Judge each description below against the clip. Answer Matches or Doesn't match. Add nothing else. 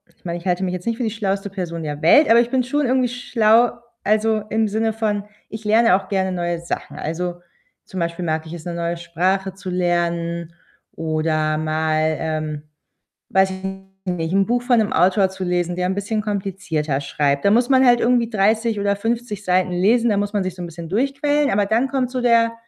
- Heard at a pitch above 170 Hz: Matches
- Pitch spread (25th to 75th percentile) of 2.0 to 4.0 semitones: Doesn't match